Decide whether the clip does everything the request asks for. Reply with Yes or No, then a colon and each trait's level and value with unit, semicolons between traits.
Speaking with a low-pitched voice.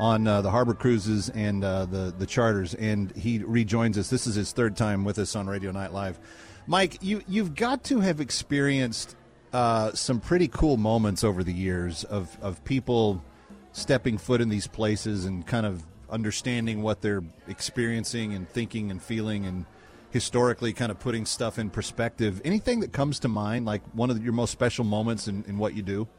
Yes: low, 110 Hz